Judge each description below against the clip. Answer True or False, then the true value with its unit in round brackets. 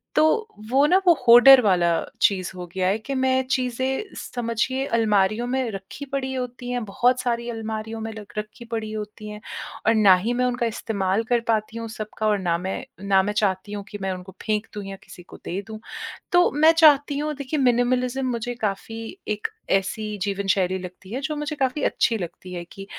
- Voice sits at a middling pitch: False (225 Hz)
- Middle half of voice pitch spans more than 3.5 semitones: True (4.2 semitones)